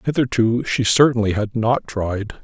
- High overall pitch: No, low, 115 Hz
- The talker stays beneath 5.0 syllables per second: Yes, 4.5 syllables/s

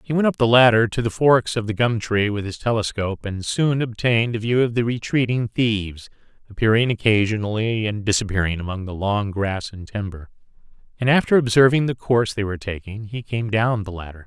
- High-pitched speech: No, low, 110 Hz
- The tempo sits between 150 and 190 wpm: No, average, 200 wpm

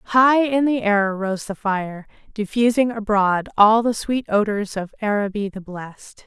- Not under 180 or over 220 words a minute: No, average, 165 wpm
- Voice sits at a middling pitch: No, high, 210 Hz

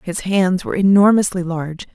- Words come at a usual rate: Yes, average, 155 wpm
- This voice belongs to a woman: Yes, female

